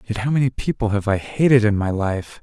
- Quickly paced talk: Yes, fast, 245 wpm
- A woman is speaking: No, male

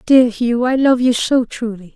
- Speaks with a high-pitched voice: Yes, high, 240 Hz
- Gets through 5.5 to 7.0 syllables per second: No, 4.4 syllables/s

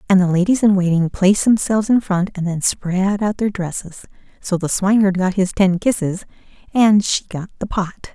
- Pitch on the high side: Yes, high, 195 Hz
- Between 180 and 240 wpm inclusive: Yes, average, 200 wpm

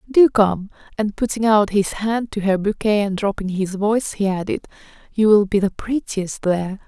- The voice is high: Yes, high, 205 Hz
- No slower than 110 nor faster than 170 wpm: No, average, 190 wpm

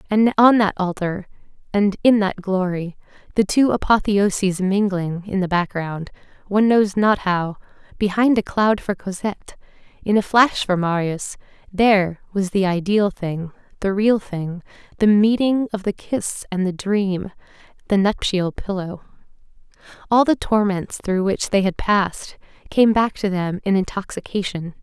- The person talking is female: Yes, female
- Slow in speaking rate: No, average, 150 wpm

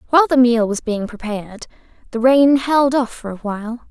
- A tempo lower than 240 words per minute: Yes, average, 200 wpm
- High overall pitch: Yes, high, 240 Hz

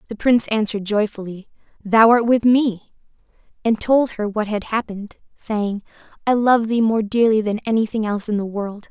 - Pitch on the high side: Yes, high, 215 Hz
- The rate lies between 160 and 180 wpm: Yes, average, 175 wpm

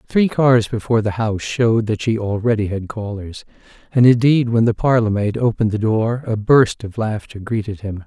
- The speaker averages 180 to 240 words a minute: Yes, average, 195 wpm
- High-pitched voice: No, low, 110 Hz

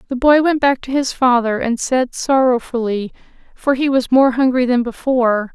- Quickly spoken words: No, average, 185 wpm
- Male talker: No, female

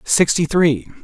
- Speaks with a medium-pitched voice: Yes, medium, 160 Hz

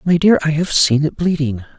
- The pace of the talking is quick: Yes, fast, 235 wpm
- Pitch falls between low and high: Yes, medium, 155 Hz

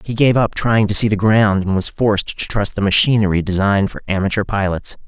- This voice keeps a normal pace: No, fast, 225 wpm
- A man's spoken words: Yes, male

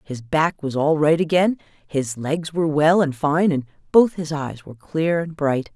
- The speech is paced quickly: Yes, fast, 210 wpm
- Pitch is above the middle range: No, medium, 155 Hz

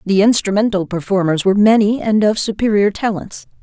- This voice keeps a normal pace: Yes, average, 150 wpm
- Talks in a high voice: Yes, high, 205 Hz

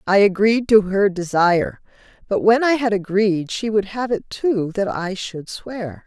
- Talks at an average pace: Yes, average, 190 wpm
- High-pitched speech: Yes, high, 200 Hz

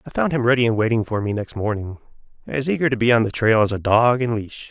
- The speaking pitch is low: Yes, low, 115 Hz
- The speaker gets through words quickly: Yes, fast, 280 wpm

